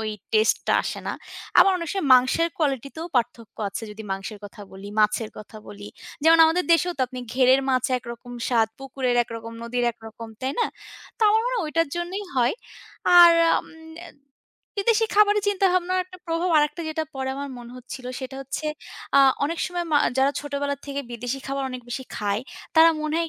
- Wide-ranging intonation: Yes, wide, 5.9 semitones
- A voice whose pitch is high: Yes, very high, 270 Hz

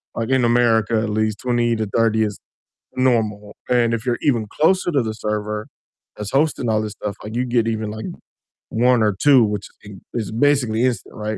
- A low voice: Yes, low, 115 Hz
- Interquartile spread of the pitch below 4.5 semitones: Yes, narrow, 2.4 semitones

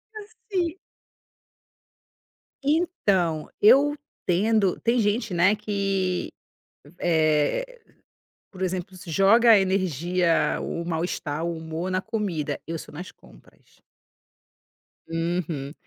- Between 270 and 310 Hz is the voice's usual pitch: No, medium, 185 Hz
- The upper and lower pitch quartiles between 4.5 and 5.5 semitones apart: Yes, average, 4.9 semitones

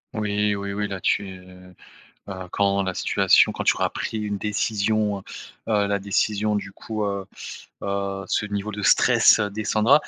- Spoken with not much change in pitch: Yes, narrow, 1.2 semitones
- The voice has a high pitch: No, low, 100 Hz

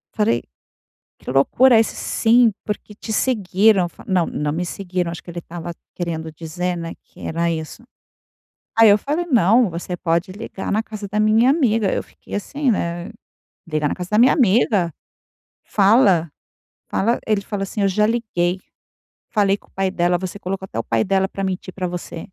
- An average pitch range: Yes, average, 3.9 semitones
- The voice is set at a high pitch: Yes, high, 195 Hz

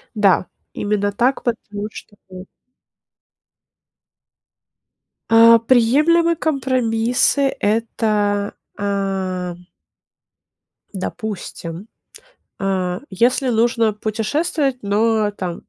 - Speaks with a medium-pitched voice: No, high, 215 Hz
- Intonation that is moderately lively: Yes, average, 3.2 semitones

